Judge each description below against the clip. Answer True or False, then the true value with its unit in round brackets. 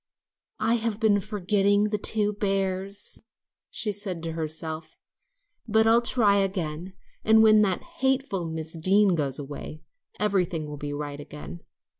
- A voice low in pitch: False (195 Hz)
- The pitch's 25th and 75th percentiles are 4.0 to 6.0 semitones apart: True (4.7 semitones)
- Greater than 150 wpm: False (135 wpm)